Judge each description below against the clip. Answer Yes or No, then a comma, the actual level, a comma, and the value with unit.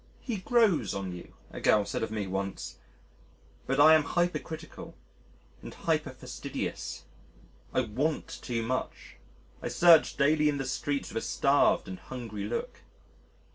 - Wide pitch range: Yes, wide, 6.7 semitones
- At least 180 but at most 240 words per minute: No, average, 140 wpm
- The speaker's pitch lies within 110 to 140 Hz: Yes, low, 135 Hz